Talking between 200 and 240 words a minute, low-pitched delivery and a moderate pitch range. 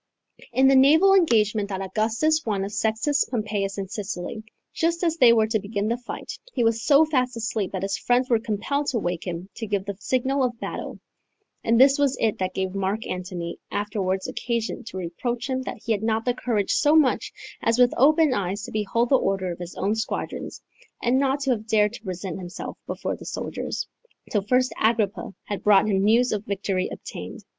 No: fast, 205 wpm; high, 220 Hz; average, 4.2 semitones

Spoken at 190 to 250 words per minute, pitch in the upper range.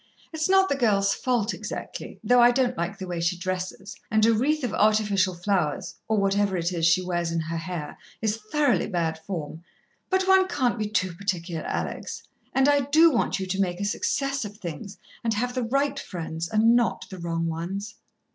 Yes: average, 200 wpm; high, 200 Hz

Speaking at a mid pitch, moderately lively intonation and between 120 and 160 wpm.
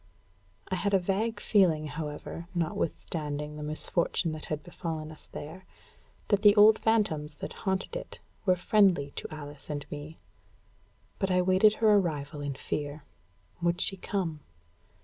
Yes: medium, 170 Hz; average, 4.4 semitones; average, 150 wpm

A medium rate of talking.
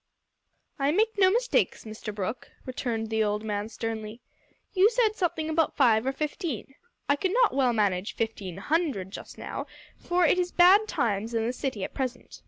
Yes: average, 180 wpm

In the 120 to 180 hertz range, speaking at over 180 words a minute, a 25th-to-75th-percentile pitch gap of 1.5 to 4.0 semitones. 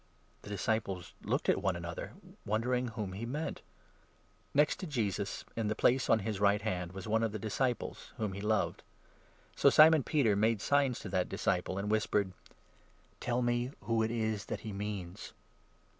No: low, 110 Hz; average, 190 wpm; average, 3.3 semitones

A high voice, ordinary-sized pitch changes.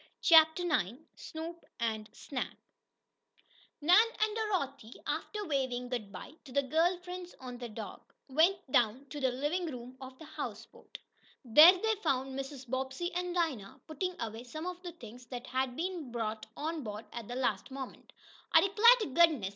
No: very high, 275 Hz; wide, 6.0 semitones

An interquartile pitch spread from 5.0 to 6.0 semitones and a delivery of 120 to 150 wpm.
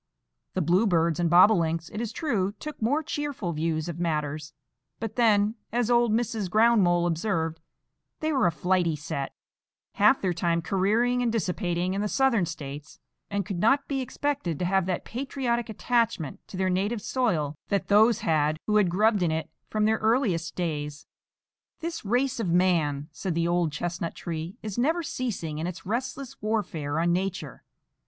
No: wide, 5.5 semitones; average, 165 wpm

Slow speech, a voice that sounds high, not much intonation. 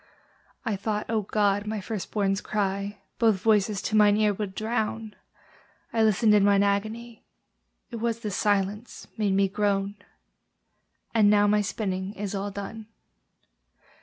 No: average, 145 wpm; high, 210 Hz; narrow, 1.6 semitones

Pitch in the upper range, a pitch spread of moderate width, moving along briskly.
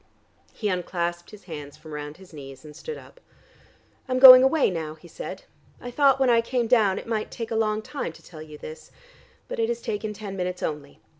No: high, 200 Hz; wide, 7.6 semitones; fast, 215 wpm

